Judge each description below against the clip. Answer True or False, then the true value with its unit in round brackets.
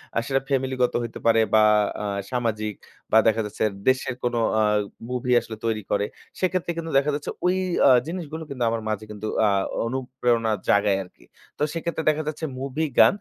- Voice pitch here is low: True (125 Hz)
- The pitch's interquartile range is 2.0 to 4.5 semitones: False (5.1 semitones)